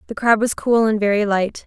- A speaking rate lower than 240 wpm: No, fast, 250 wpm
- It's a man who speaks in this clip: No, female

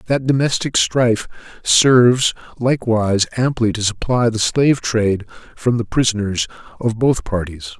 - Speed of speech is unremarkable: No, slow, 130 wpm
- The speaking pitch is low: Yes, low, 115 Hz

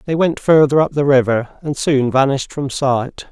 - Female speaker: No, male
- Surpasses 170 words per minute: Yes, average, 200 wpm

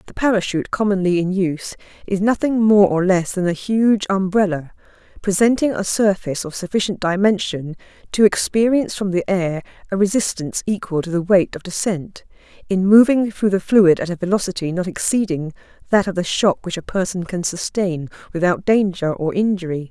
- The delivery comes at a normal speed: Yes, average, 170 wpm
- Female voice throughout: Yes, female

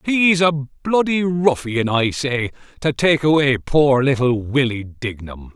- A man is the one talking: Yes, male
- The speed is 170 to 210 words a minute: No, average, 140 wpm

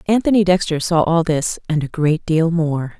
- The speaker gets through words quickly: No, average, 180 wpm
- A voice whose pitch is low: No, medium, 165 Hz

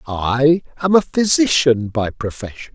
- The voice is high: No, medium, 140 Hz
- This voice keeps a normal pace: No, slow, 130 wpm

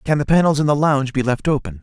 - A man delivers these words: Yes, male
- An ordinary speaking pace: No, fast, 295 wpm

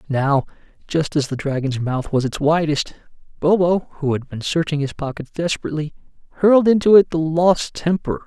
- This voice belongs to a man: Yes, male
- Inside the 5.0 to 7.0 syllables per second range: Yes, 5.2 syllables/s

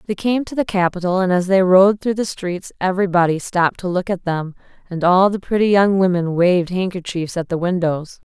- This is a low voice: No, medium, 185 Hz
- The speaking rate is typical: No, fast, 210 wpm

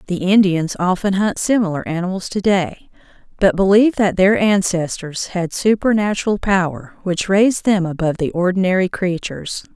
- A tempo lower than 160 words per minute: Yes, average, 140 wpm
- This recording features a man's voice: No, female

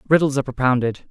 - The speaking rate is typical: Yes, average, 160 wpm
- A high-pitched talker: No, low, 135 Hz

